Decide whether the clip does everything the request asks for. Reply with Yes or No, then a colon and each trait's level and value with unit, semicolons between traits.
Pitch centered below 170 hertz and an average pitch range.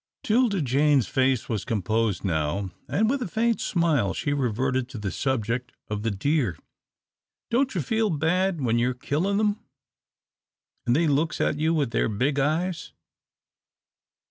No: medium, 140 Hz; wide, 6.9 semitones